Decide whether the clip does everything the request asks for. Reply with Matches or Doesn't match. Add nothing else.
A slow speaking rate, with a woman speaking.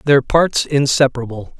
Doesn't match